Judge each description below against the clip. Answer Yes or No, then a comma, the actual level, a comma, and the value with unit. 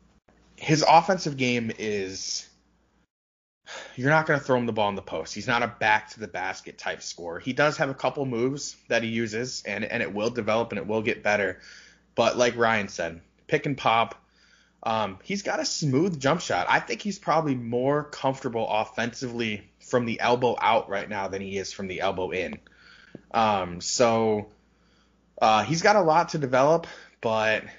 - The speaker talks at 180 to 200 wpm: Yes, average, 190 wpm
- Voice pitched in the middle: No, low, 120 Hz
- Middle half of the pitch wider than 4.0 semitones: Yes, average, 4.7 semitones